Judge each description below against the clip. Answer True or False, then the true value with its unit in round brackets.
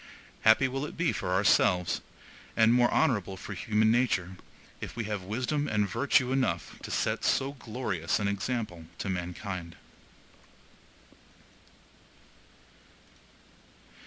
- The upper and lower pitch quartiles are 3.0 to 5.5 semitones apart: True (5.2 semitones)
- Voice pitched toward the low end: True (110 Hz)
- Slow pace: True (115 wpm)